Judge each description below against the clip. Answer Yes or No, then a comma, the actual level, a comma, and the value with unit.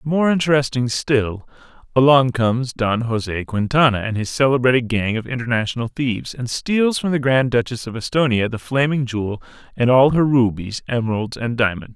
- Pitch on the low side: Yes, low, 125 Hz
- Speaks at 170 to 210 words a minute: No, average, 160 wpm